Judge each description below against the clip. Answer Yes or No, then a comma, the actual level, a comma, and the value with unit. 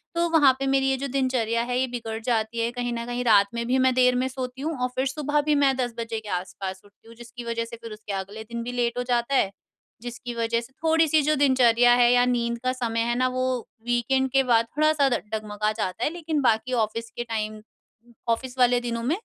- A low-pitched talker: No, high, 245 Hz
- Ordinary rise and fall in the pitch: No, narrow, 2.3 semitones